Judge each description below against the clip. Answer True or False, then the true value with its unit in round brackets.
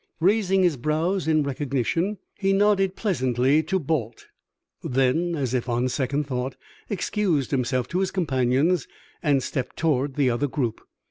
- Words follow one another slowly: False (145 wpm)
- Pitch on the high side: False (145 Hz)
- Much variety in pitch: True (5.8 semitones)